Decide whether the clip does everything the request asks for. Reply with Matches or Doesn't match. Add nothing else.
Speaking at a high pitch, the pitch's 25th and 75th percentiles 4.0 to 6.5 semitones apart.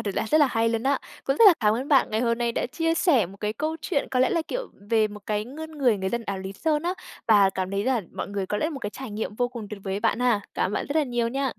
Matches